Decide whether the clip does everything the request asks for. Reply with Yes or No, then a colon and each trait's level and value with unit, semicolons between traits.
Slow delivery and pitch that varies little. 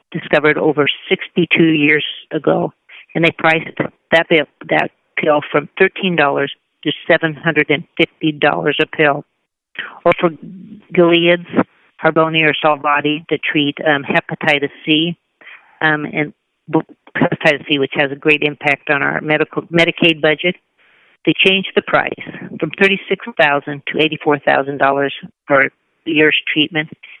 Yes: slow, 115 wpm; narrow, 2.3 semitones